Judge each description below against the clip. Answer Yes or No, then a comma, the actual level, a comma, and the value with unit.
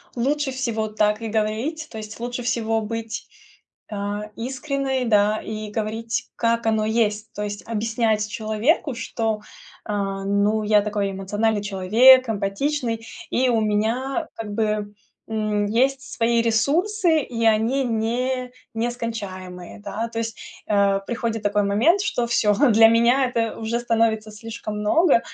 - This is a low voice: No, high, 225 Hz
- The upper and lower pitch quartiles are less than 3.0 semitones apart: Yes, narrow, 2.4 semitones